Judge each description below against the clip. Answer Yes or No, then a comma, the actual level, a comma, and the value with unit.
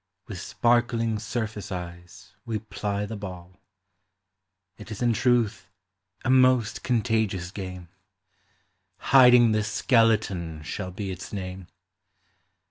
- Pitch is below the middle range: Yes, low, 105 Hz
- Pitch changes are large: No, average, 3.9 semitones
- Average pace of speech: No, slow, 115 wpm